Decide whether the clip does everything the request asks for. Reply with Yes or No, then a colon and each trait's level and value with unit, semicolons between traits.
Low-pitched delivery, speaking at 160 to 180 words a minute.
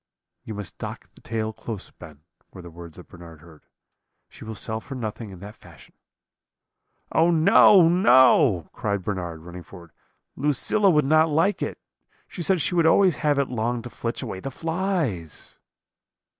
Yes: low, 115 Hz; average, 170 wpm